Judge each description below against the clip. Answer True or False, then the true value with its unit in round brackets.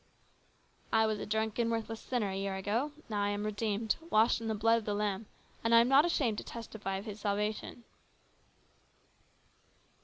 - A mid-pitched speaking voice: False (220 Hz)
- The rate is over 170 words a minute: True (185 wpm)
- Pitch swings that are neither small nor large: False (1.9 semitones)